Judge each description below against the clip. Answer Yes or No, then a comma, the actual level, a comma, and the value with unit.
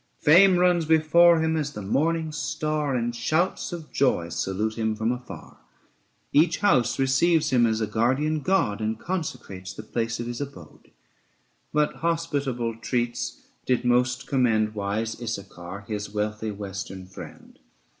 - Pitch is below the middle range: Yes, low, 120 Hz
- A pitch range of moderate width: No, wide, 6.1 semitones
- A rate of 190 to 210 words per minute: No, average, 145 wpm